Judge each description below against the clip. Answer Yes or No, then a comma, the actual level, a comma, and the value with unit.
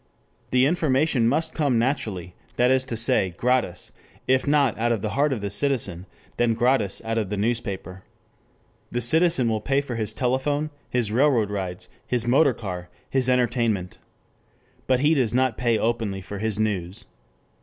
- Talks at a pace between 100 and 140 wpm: No, average, 165 wpm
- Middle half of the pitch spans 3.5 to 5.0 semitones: Yes, average, 3.9 semitones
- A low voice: Yes, low, 120 Hz